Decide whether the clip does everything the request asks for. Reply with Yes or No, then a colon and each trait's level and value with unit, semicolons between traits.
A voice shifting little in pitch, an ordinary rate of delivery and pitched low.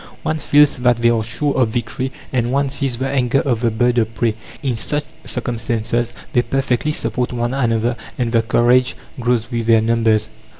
Yes: narrow, 2.3 semitones; average, 185 wpm; low, 120 Hz